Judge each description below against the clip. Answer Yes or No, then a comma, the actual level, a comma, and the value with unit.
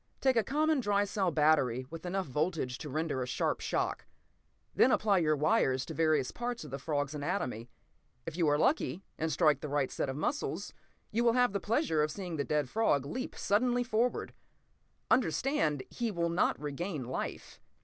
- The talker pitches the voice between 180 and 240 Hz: No, medium, 165 Hz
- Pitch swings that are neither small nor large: No, wide, 6.9 semitones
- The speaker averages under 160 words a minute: No, average, 185 wpm